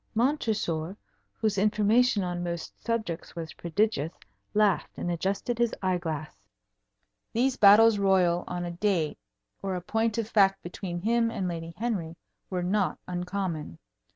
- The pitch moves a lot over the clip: No, average, 4.0 semitones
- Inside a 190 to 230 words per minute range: No, average, 140 wpm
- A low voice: No, high, 190 Hz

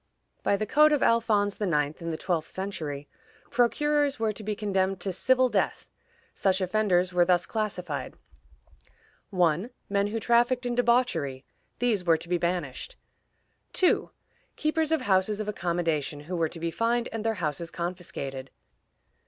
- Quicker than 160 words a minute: No, average, 155 wpm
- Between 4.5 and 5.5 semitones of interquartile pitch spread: Yes, average, 5.1 semitones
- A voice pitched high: Yes, high, 195 Hz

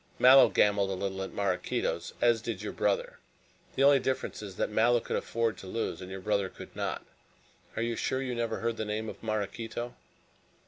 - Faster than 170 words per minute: Yes, average, 195 wpm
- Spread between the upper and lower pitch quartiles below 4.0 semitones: Yes, average, 2.9 semitones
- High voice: No, low, 110 Hz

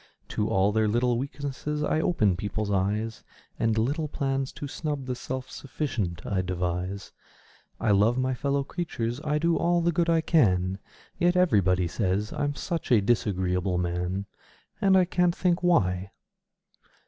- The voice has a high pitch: No, low, 120 Hz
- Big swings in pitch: Yes, wide, 7.6 semitones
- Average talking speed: Yes, average, 155 wpm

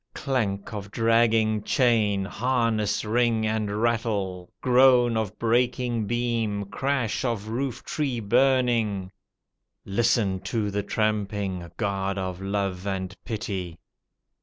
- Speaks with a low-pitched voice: Yes, low, 110 Hz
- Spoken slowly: Yes, slow, 110 wpm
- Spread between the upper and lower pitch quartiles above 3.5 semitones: No, average, 3.0 semitones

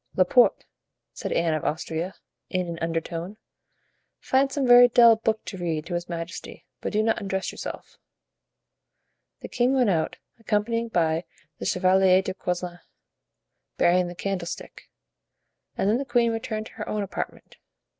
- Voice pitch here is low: No, high, 190 Hz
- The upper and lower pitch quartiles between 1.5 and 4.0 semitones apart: No, average, 4.6 semitones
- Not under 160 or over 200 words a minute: No, average, 150 wpm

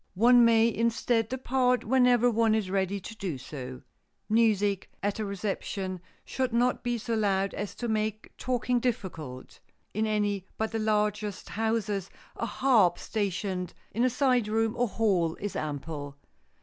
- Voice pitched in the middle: No, high, 215 Hz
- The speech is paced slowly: No, average, 150 wpm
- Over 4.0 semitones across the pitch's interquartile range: No, average, 3.2 semitones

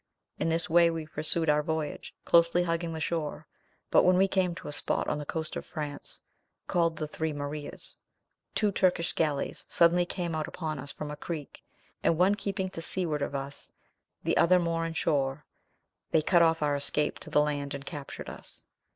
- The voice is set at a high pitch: No, medium, 160 Hz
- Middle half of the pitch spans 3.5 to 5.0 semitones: No, narrow, 2.5 semitones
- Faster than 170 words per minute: Yes, average, 195 wpm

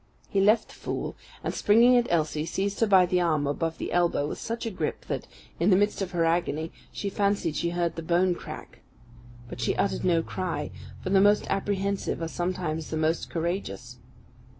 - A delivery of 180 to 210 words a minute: Yes, average, 195 wpm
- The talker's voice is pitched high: No, medium, 175 Hz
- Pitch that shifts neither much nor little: Yes, average, 3.3 semitones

